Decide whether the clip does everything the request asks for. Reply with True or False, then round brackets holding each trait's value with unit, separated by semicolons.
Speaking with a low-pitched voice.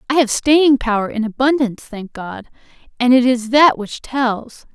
False (245 Hz)